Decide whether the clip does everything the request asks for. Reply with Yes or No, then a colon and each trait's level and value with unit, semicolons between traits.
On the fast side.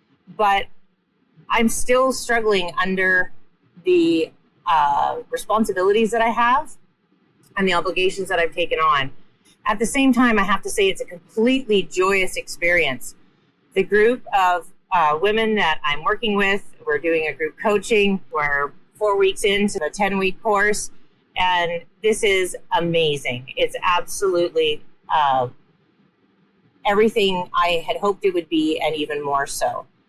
No: average, 140 wpm